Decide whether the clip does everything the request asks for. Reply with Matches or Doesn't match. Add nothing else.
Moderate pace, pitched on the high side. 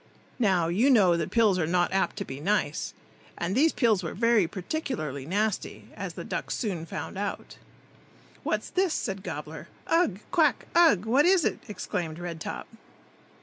Matches